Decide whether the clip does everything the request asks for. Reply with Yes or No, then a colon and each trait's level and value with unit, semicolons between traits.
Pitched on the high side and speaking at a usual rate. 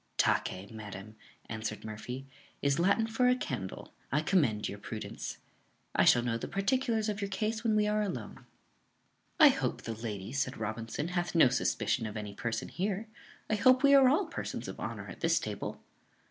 No: medium, 145 Hz; average, 180 wpm